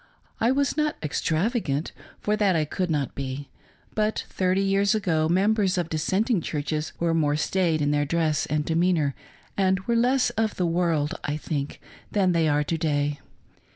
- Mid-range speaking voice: Yes, medium, 170 Hz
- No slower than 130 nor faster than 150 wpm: No, average, 170 wpm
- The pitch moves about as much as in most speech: Yes, average, 4.7 semitones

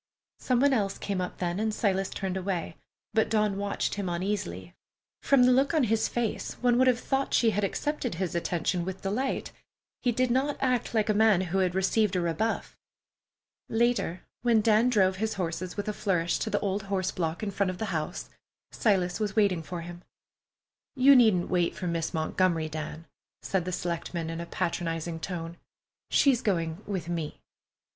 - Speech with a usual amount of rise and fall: Yes, average, 4.3 semitones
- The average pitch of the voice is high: Yes, high, 195 Hz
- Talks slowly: No, average, 185 wpm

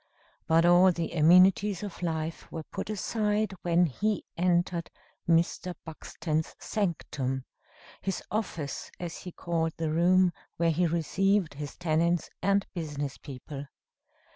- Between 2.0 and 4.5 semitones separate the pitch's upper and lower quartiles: Yes, narrow, 2.6 semitones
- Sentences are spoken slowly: Yes, slow, 125 wpm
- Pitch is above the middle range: No, medium, 170 Hz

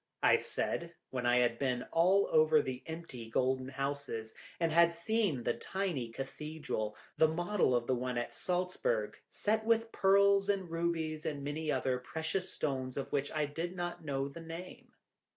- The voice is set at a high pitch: No, medium, 155 Hz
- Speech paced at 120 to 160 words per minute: No, average, 170 wpm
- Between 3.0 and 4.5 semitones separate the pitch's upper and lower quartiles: No, average, 5.1 semitones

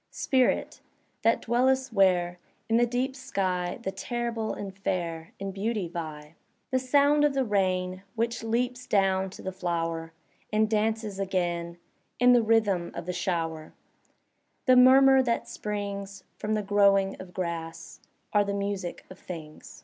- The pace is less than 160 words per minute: Yes, average, 150 wpm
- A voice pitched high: Yes, high, 200 Hz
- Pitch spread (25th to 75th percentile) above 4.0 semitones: Yes, average, 4.7 semitones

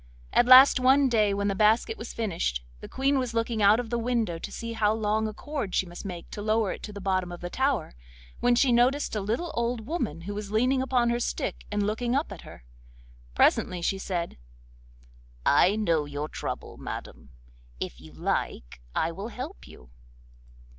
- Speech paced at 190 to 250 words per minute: Yes, average, 195 wpm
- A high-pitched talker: Yes, high, 215 Hz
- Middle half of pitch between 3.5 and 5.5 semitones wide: Yes, average, 4.5 semitones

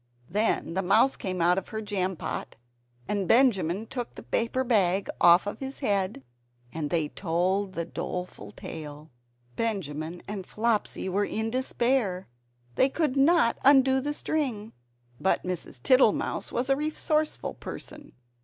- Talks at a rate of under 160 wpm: Yes, average, 140 wpm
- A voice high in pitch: Yes, high, 205 Hz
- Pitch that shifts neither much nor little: No, wide, 6.3 semitones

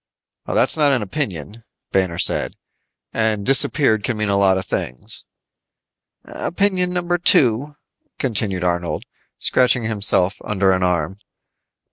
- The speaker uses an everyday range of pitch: No, wide, 6.1 semitones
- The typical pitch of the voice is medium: No, low, 105 Hz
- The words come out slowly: Yes, slow, 120 wpm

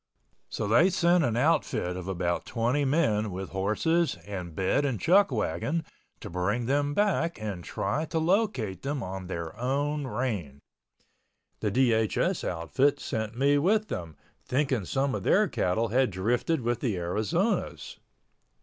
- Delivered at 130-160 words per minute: Yes, average, 145 wpm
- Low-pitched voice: Yes, low, 120 Hz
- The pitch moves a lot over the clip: Yes, wide, 7.3 semitones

